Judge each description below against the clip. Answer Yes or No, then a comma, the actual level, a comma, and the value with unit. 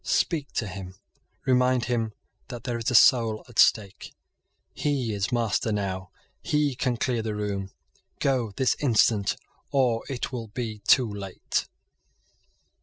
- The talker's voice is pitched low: Yes, low, 115 Hz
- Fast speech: No, average, 140 wpm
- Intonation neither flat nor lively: Yes, average, 3.4 semitones